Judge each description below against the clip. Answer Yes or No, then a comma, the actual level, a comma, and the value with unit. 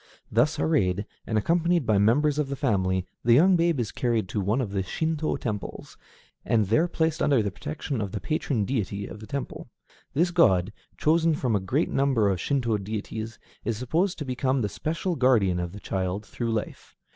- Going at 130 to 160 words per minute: No, average, 190 wpm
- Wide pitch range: Yes, wide, 6.6 semitones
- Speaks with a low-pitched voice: Yes, low, 115 Hz